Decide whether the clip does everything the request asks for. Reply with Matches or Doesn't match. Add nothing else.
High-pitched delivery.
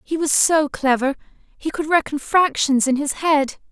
Matches